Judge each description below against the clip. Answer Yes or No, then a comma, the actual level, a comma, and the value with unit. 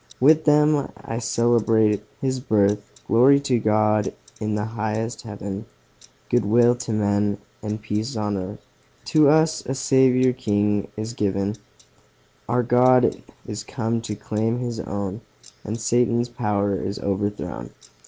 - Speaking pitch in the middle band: No, low, 110 Hz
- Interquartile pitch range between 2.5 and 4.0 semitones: Yes, average, 2.9 semitones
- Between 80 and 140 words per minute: Yes, slow, 135 wpm